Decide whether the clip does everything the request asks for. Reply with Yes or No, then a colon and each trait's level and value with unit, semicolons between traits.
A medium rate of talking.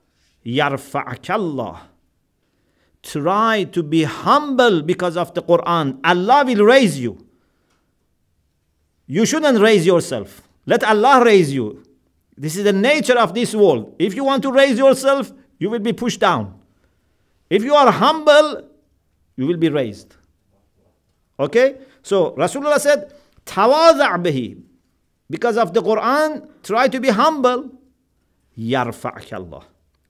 No: slow, 120 wpm